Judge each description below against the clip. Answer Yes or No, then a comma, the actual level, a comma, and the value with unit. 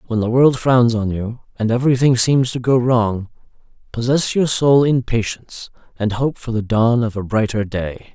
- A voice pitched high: No, low, 120 Hz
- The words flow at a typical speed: Yes, average, 190 wpm